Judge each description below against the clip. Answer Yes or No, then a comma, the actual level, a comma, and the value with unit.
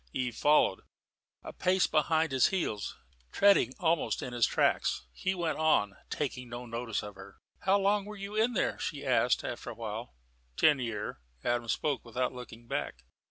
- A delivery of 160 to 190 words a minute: Yes, average, 170 wpm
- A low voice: Yes, low, 130 Hz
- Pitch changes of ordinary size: No, wide, 7.4 semitones